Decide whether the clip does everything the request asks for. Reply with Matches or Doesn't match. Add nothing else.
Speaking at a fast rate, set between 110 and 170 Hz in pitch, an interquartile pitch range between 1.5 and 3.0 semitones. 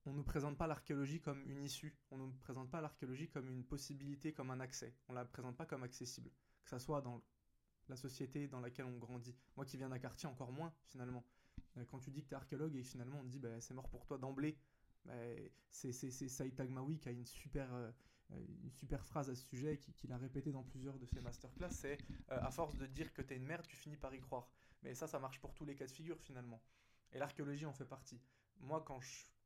Matches